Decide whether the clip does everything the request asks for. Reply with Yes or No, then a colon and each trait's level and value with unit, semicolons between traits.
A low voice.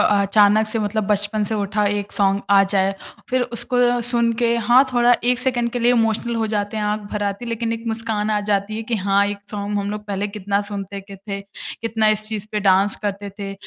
No: high, 210 Hz